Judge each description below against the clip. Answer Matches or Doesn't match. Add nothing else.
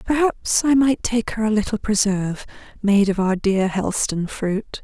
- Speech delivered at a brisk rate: Doesn't match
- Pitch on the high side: Matches